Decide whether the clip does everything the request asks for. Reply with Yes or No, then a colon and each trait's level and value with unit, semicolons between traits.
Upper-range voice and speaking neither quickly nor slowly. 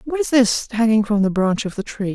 No: high, 220 Hz; fast, 280 wpm